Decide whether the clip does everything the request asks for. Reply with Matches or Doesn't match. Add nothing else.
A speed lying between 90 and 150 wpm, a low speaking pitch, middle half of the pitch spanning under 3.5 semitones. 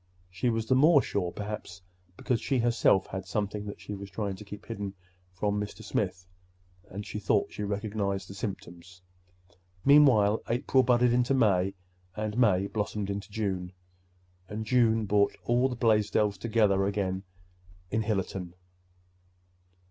Matches